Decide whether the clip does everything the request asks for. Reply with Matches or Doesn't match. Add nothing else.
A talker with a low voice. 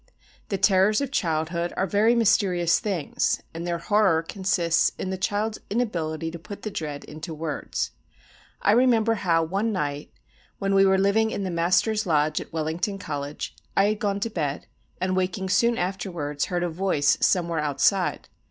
Doesn't match